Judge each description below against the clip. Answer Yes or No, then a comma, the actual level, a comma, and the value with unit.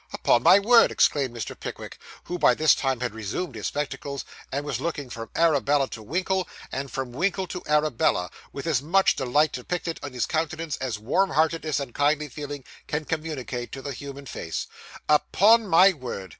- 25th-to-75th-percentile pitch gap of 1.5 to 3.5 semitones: No, average, 4.2 semitones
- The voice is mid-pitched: Yes, medium, 145 Hz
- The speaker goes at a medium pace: Yes, average, 175 wpm